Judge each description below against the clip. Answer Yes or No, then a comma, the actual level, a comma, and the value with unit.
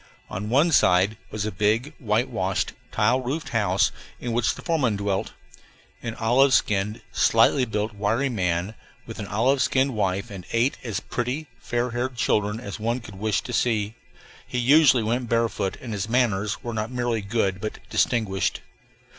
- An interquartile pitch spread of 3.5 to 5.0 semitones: No, average, 3.1 semitones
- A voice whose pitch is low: Yes, low, 115 Hz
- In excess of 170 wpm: No, average, 165 wpm